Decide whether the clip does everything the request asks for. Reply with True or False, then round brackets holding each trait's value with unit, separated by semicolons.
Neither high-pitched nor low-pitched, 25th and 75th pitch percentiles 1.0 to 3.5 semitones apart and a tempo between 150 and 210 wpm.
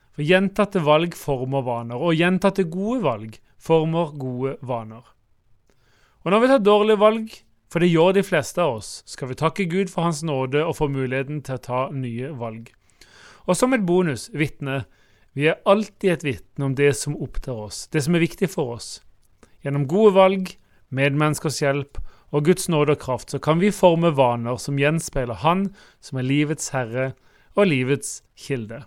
False (145 Hz; 5.4 semitones; 175 wpm)